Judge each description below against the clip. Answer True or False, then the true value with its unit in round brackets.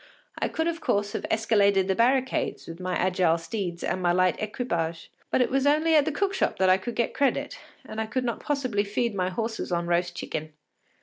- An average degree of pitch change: False (5.8 semitones)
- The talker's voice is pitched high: True (205 Hz)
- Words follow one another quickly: True (220 wpm)